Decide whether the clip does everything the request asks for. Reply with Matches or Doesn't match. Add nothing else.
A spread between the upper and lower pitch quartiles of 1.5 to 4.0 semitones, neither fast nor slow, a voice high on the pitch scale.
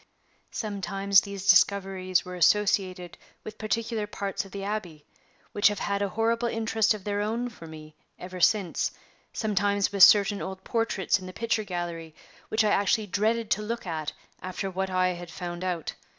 Matches